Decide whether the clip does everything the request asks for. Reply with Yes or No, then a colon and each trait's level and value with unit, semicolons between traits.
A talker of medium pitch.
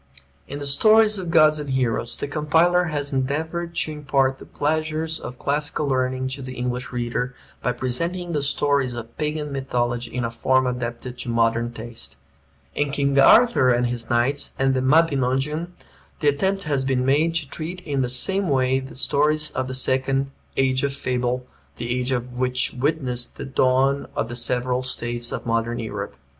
No: low, 130 Hz